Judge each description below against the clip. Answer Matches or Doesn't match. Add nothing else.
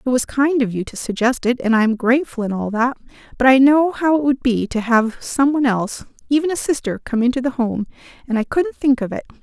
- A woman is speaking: Matches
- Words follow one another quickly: Matches